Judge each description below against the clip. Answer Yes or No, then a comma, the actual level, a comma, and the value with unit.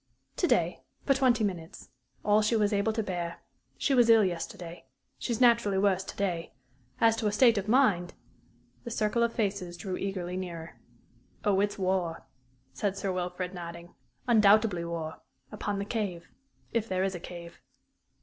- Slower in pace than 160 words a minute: No, average, 170 wpm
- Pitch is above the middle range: Yes, high, 195 Hz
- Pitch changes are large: No, average, 3.6 semitones